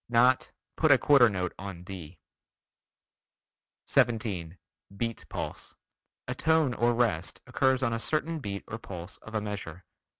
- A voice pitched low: Yes, low, 115 Hz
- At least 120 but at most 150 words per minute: Yes, average, 140 wpm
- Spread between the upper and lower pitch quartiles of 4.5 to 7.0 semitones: Yes, wide, 5.4 semitones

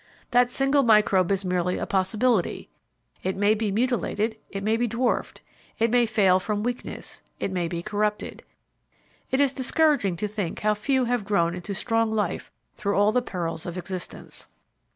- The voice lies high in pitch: Yes, high, 210 Hz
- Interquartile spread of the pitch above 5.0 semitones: No, average, 4.1 semitones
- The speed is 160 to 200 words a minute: Yes, average, 170 wpm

